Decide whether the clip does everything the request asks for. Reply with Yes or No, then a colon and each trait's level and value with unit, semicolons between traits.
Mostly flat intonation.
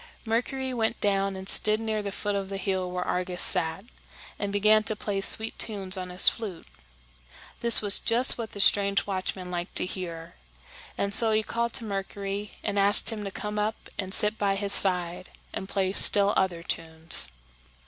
Yes: narrow, 2.3 semitones